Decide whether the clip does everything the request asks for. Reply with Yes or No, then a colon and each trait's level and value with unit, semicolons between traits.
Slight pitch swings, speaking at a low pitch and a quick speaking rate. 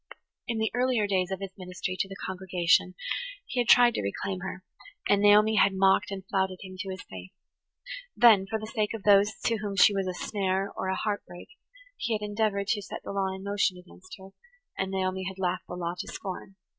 No: narrow, 1.8 semitones; high, 195 Hz; fast, 220 wpm